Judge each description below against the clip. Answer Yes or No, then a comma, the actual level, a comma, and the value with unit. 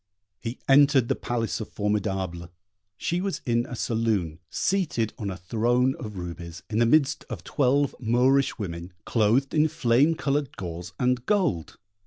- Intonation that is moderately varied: No, wide, 6.1 semitones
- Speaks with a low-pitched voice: Yes, low, 115 Hz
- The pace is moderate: Yes, average, 155 wpm